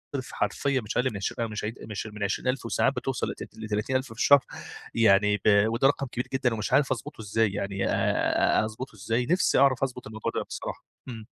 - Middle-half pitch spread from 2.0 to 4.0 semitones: Yes, average, 3.6 semitones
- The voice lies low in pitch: Yes, low, 115 Hz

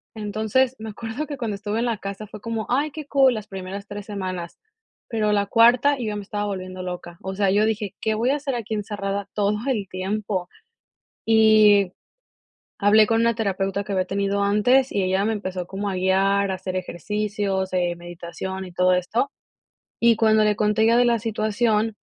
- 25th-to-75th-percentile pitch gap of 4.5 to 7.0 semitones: No, narrow, 2.6 semitones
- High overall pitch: Yes, high, 205 Hz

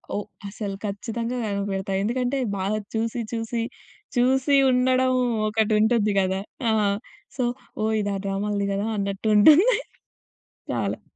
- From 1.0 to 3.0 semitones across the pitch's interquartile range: No, average, 3.5 semitones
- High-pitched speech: Yes, high, 220 Hz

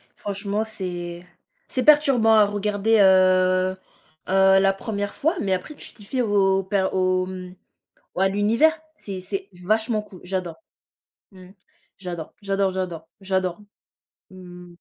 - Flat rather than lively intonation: Yes, narrow, 2.3 semitones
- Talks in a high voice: Yes, high, 195 Hz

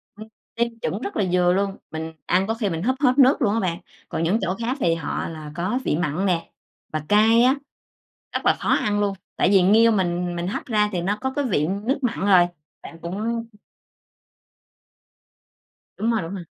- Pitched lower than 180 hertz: No, high, 200 Hz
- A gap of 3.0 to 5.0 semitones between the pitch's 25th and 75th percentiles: Yes, average, 4.7 semitones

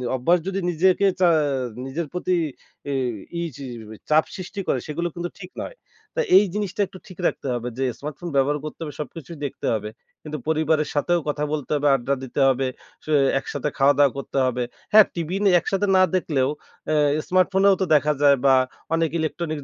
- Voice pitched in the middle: Yes, medium, 155 Hz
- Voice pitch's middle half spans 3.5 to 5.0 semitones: Yes, average, 4.5 semitones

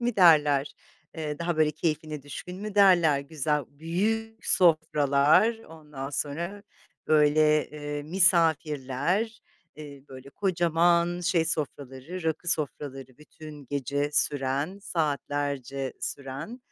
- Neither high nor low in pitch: Yes, medium, 155 Hz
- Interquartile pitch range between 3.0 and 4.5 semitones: Yes, average, 3.4 semitones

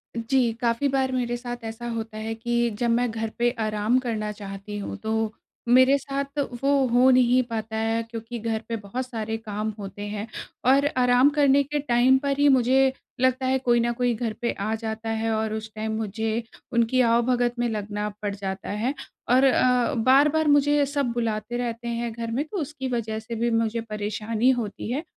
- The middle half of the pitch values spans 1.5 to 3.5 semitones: Yes, narrow, 2.6 semitones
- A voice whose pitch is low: No, high, 235 Hz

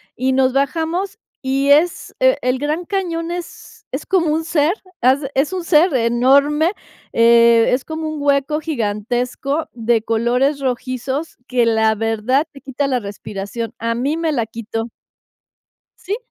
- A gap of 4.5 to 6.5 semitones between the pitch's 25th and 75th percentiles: Yes, average, 5.0 semitones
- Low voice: No, very high, 270 Hz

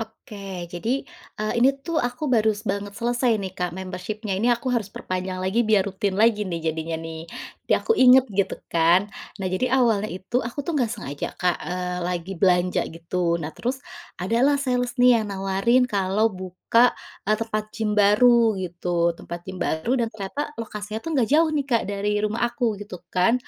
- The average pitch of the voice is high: Yes, high, 210 Hz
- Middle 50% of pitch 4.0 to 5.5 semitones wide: Yes, average, 4.5 semitones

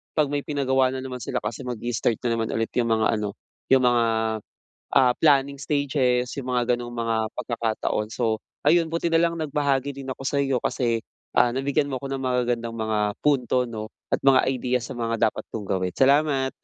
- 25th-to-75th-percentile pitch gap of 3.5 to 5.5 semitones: No, average, 3.1 semitones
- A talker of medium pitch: No, low, 125 Hz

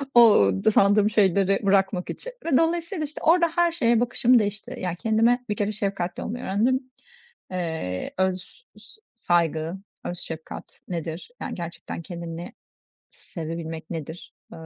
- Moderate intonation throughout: No, wide, 5.9 semitones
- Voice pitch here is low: No, high, 195 Hz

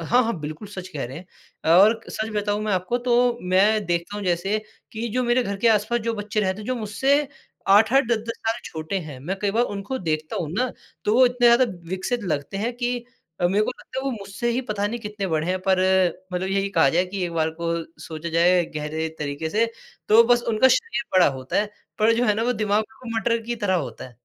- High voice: Yes, high, 205 Hz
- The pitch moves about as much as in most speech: Yes, average, 4.6 semitones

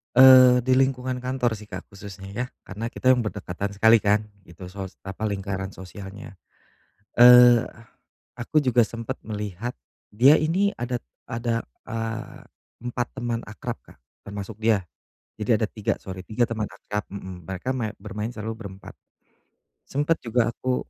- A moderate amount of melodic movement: Yes, average, 3.5 semitones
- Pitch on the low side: Yes, low, 115 Hz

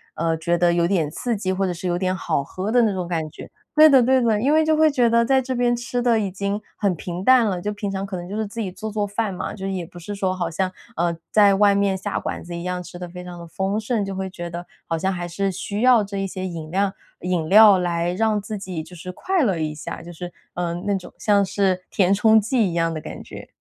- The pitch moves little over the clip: No, average, 3.4 semitones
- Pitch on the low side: No, high, 190 Hz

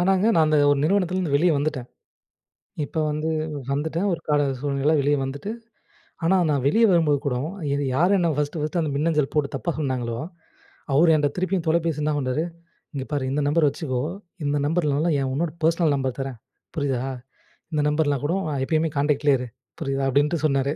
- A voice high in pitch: No, medium, 150 Hz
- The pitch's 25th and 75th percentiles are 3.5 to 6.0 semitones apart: No, average, 2.8 semitones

